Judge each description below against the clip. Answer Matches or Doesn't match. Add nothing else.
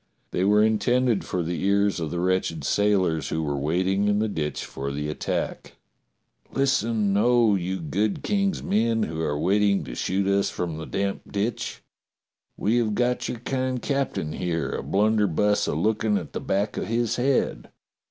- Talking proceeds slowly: Doesn't match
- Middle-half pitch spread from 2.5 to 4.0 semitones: Doesn't match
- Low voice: Matches